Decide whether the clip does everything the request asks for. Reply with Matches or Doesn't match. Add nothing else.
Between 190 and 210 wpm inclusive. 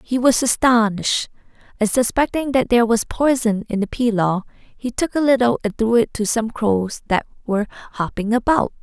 Doesn't match